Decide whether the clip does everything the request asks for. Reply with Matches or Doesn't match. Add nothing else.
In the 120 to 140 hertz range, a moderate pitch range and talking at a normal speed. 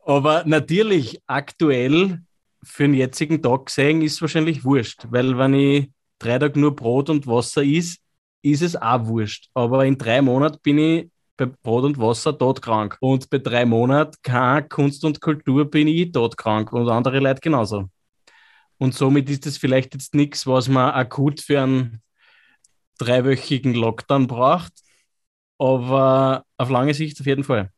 Matches